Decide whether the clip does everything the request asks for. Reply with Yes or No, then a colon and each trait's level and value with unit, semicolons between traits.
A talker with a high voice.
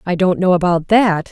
No: medium, 180 Hz